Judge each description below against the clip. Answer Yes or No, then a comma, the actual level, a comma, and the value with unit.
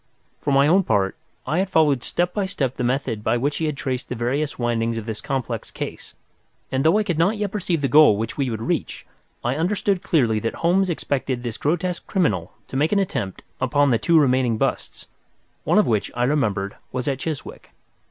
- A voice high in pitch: No, low, 135 Hz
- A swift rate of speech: Yes, fast, 210 wpm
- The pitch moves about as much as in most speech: No, wide, 5.7 semitones